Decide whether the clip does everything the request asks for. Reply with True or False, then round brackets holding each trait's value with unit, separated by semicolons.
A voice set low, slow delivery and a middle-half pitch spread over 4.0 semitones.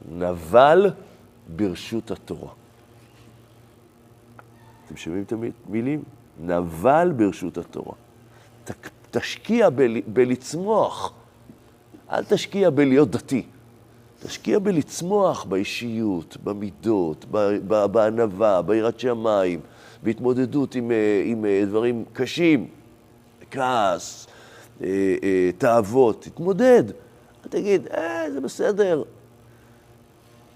False (120 Hz; 75 wpm; 2.9 semitones)